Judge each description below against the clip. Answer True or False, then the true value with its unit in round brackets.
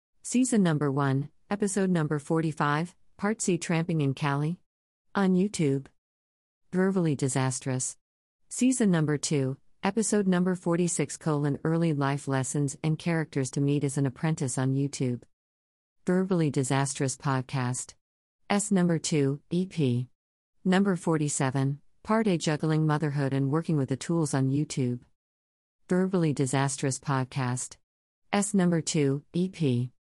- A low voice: False (145 Hz)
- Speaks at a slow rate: True (120 wpm)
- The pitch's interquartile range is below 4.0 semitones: False (4.3 semitones)